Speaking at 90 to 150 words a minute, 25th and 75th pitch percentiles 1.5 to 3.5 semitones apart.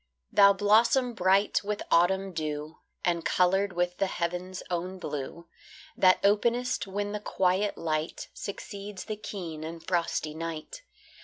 Yes: slow, 135 wpm; average, 3.2 semitones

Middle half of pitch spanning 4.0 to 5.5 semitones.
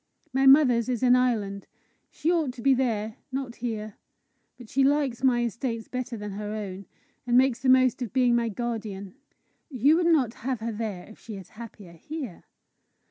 No: average, 3.3 semitones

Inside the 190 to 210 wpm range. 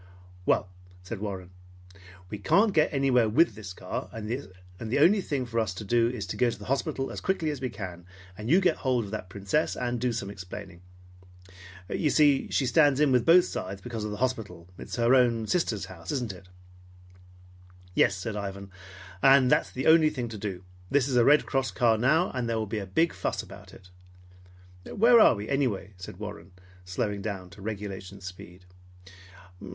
Yes: average, 195 wpm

